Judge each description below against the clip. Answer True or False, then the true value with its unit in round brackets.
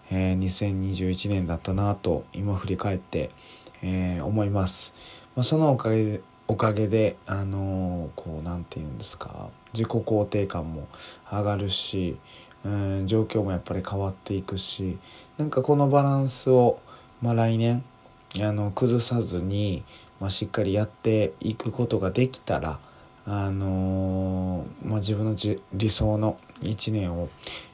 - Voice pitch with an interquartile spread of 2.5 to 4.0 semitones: True (2.9 semitones)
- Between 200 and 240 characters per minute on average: True (230 characters per minute)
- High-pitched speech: False (100 Hz)